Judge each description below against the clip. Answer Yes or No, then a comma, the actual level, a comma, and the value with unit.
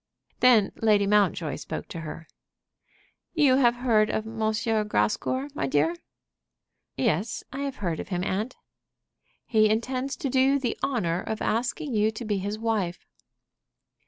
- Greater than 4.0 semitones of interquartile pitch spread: Yes, average, 4.4 semitones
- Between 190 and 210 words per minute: No, average, 150 wpm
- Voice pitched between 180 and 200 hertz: No, high, 220 Hz